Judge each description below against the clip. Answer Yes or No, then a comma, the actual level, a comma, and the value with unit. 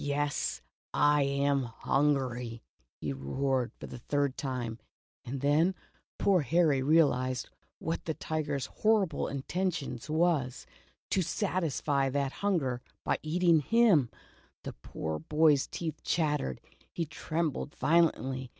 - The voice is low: No, medium, 145 Hz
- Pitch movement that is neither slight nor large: Yes, average, 3.8 semitones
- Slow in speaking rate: Yes, slow, 125 wpm